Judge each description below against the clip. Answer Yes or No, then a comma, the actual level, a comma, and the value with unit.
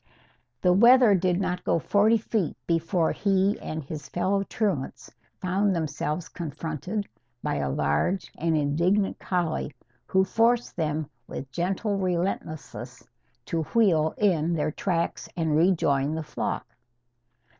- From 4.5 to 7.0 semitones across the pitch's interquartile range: No, average, 4.0 semitones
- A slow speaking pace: Yes, slow, 125 wpm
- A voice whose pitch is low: No, medium, 175 Hz